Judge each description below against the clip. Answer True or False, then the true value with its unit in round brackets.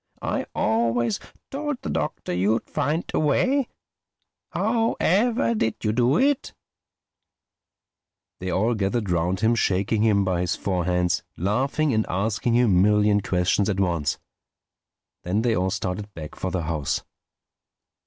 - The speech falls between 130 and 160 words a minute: True (145 wpm)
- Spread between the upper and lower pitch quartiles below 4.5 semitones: False (5.0 semitones)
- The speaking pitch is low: True (105 Hz)